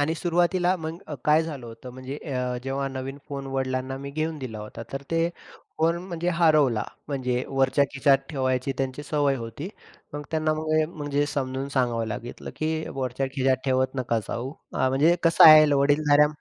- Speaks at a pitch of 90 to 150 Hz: Yes, medium, 140 Hz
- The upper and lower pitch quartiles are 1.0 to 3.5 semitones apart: Yes, average, 3.1 semitones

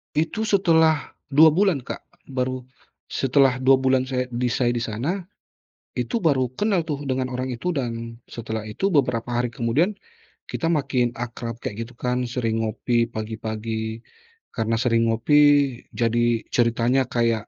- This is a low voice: Yes, low, 125 Hz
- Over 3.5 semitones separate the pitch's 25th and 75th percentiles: No, average, 3.2 semitones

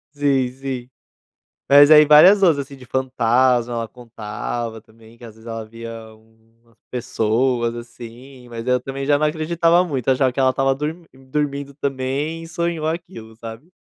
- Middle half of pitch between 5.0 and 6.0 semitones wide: No, average, 4.0 semitones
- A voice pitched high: No, low, 130 Hz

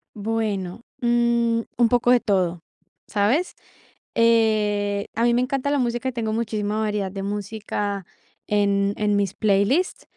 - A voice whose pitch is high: Yes, high, 215 Hz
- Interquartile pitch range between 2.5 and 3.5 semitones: Yes, average, 2.8 semitones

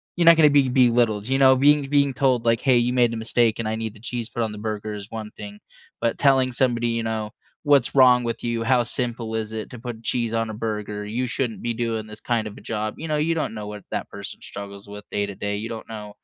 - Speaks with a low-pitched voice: Yes, low, 115 Hz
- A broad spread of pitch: No, average, 2.7 semitones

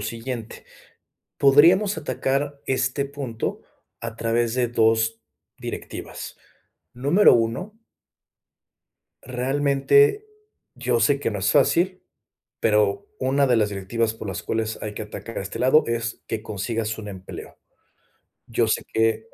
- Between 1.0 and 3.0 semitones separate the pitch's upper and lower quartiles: No, average, 3.9 semitones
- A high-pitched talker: No, low, 115 Hz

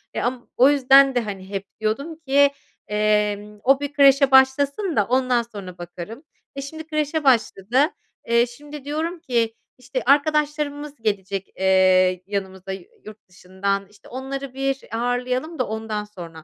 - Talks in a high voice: Yes, high, 245 Hz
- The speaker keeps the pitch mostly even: No, wide, 5.4 semitones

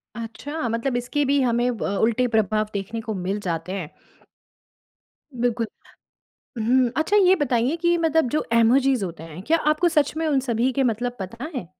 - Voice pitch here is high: Yes, high, 245 Hz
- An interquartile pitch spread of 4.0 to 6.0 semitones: Yes, average, 4.8 semitones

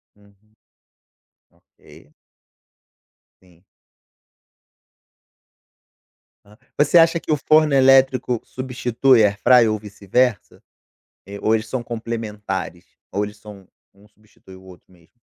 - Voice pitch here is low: Yes, low, 110 Hz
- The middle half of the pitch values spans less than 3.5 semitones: No, average, 4.2 semitones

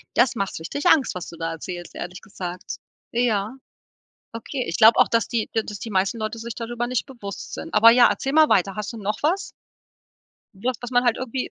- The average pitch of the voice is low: No, high, 225 Hz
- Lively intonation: No, average, 3.8 semitones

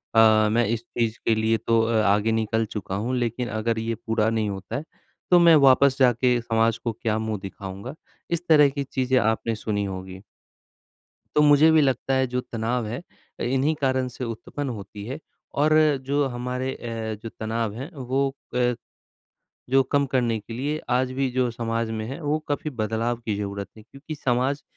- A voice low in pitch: Yes, low, 120 Hz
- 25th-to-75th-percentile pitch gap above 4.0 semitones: No, average, 3.1 semitones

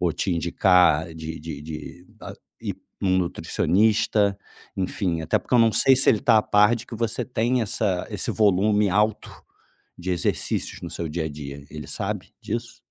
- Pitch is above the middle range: No, very low, 95 Hz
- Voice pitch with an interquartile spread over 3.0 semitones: Yes, average, 4.7 semitones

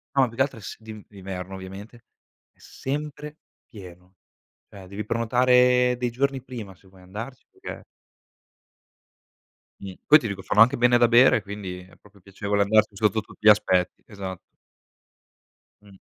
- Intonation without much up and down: No, average, 4.2 semitones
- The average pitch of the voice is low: Yes, low, 105 Hz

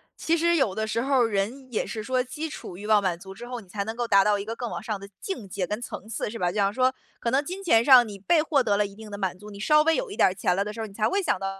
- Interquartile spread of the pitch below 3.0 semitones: No, average, 4.5 semitones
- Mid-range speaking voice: No, high, 220 Hz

